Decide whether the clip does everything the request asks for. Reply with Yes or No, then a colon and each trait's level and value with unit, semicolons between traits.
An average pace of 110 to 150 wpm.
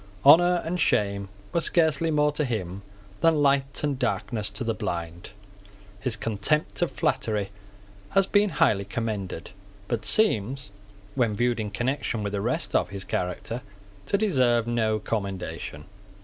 Yes: average, 145 wpm